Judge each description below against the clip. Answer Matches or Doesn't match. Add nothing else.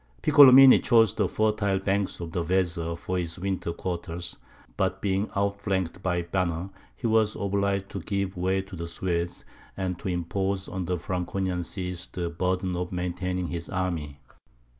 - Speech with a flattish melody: Matches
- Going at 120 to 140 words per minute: Doesn't match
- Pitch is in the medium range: Doesn't match